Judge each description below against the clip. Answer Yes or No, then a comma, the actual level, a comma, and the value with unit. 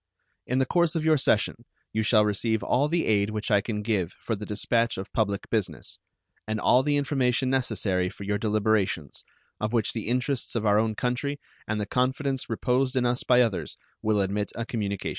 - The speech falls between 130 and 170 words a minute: No, average, 200 wpm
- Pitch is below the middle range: Yes, low, 115 Hz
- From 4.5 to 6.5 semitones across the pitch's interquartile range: No, average, 3.5 semitones